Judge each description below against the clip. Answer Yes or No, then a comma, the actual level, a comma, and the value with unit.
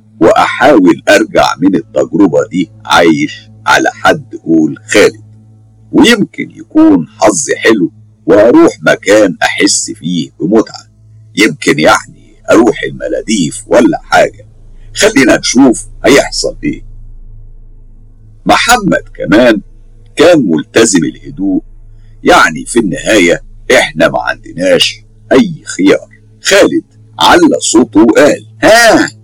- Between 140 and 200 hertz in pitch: No, low, 110 Hz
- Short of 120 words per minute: Yes, average, 95 wpm